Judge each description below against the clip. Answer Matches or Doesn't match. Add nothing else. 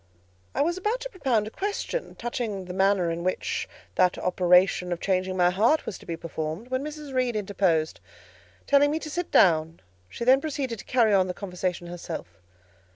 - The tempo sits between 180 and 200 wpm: Matches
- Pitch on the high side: Matches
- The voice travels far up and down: Matches